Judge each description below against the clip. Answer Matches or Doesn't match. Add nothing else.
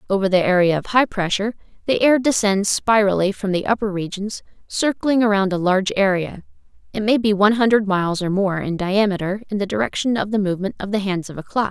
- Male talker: Doesn't match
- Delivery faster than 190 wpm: Matches